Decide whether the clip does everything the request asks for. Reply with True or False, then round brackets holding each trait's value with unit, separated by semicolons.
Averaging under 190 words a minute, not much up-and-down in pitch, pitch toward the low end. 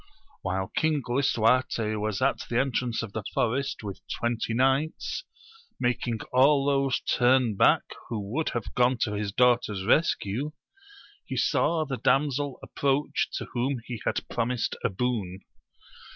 False (140 wpm; 3.7 semitones; 125 Hz)